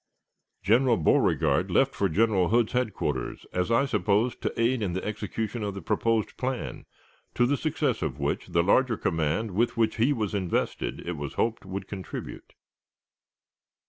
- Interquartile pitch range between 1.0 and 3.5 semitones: No, average, 4.3 semitones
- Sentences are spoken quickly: No, average, 160 wpm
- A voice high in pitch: No, low, 105 Hz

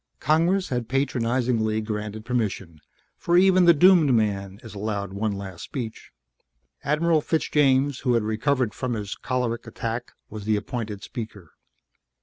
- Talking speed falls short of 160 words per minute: Yes, slow, 135 wpm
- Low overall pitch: Yes, low, 115 Hz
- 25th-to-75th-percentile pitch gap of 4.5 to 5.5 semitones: Yes, average, 4.8 semitones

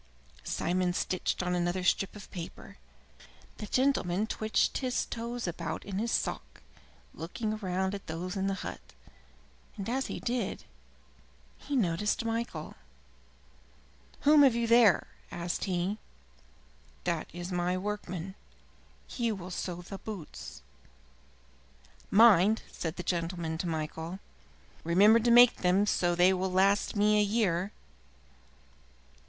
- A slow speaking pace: Yes, slow, 130 wpm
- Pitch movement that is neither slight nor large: Yes, average, 3.7 semitones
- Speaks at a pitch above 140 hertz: Yes, high, 190 Hz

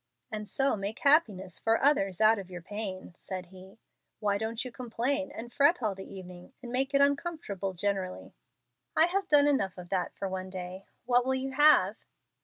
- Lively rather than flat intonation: Yes, wide, 6.1 semitones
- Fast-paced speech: No, average, 190 wpm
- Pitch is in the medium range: No, high, 215 Hz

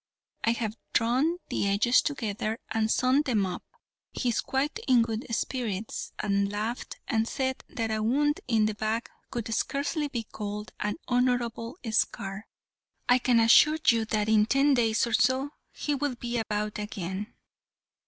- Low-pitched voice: No, high, 230 Hz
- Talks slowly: No, average, 160 wpm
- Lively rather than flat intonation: No, average, 3.0 semitones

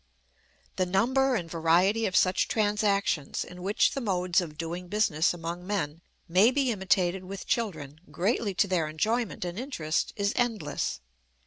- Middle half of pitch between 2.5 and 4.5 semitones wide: Yes, average, 4.0 semitones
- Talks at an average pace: Yes, average, 150 wpm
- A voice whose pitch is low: No, medium, 185 Hz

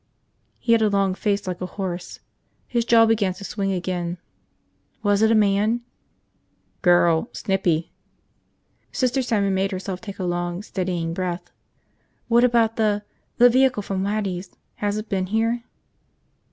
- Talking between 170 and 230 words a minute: No, average, 150 wpm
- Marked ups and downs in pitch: No, average, 3.5 semitones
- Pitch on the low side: No, high, 200 Hz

